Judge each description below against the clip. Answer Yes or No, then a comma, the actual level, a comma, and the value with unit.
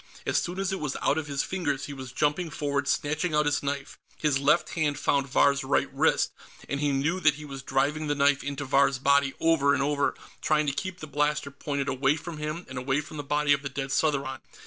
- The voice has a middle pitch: Yes, medium, 145 Hz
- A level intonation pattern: Yes, narrow, 1.5 semitones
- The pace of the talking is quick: Yes, fast, 235 wpm